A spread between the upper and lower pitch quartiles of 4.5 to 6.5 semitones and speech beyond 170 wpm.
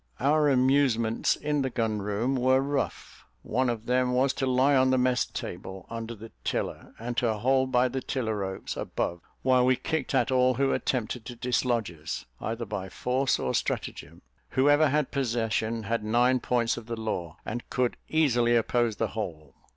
No: average, 2.7 semitones; average, 180 wpm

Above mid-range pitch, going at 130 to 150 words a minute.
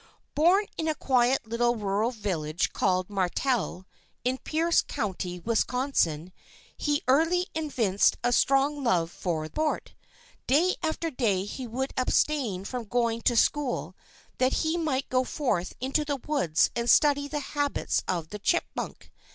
Yes: very high, 250 Hz; average, 145 wpm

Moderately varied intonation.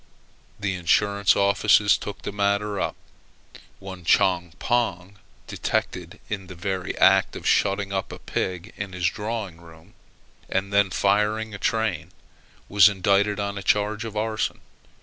No: narrow, 2.0 semitones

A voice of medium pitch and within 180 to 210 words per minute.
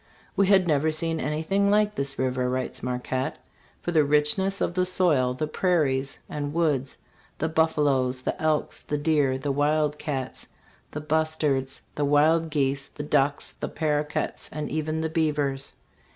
No: medium, 150 Hz; average, 165 wpm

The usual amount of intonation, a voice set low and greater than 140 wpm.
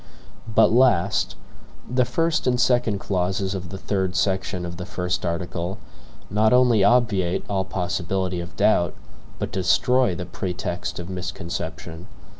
No: average, 3.6 semitones; very low, 95 Hz; slow, 135 wpm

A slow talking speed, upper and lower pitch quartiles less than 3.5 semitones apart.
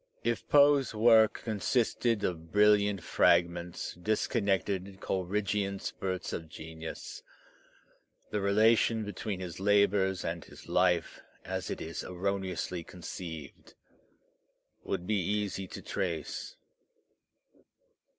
Yes: slow, 100 wpm; average, 3.0 semitones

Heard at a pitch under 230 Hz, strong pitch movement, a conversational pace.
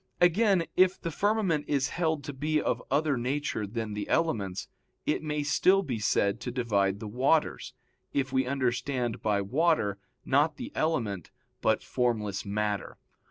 Yes: low, 135 Hz; wide, 6.8 semitones; average, 155 wpm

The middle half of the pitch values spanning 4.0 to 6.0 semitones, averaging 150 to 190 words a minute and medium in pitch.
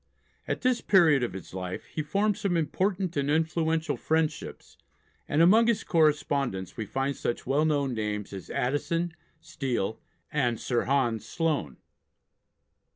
No: wide, 5.6 semitones; average, 140 wpm; medium, 145 Hz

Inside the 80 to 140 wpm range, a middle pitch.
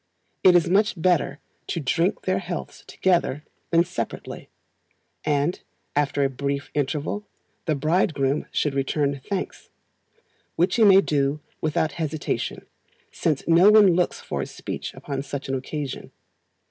Yes: slow, 135 wpm; medium, 155 Hz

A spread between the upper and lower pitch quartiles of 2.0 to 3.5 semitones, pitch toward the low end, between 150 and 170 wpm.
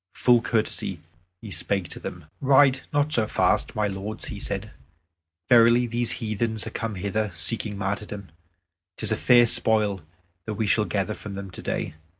Yes: average, 2.8 semitones; low, 110 Hz; average, 160 wpm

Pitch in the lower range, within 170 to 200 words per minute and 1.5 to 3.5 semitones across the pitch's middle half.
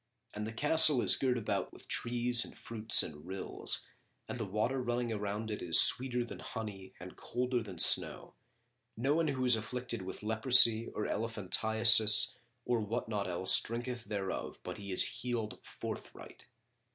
No: low, 110 Hz; average, 160 wpm; average, 2.9 semitones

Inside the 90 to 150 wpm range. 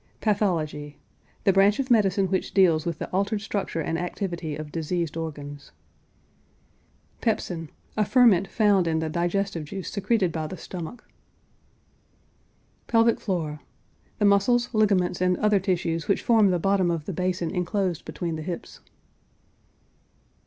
Yes: average, 140 wpm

